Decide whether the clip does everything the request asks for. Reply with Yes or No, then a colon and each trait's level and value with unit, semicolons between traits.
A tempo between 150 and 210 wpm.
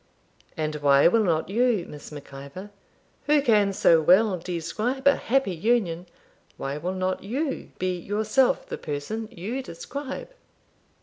No: average, 140 wpm